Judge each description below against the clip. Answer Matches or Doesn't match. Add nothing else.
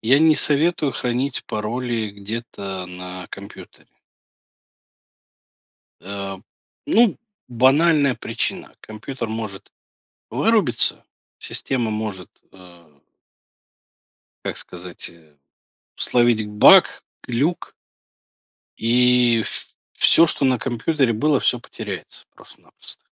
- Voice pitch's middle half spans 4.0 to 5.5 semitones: Matches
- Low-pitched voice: Matches